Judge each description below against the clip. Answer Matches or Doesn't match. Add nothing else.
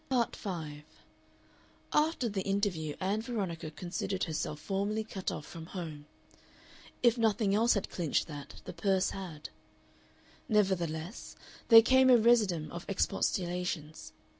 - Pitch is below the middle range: Doesn't match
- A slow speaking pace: Matches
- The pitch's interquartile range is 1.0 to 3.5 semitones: Doesn't match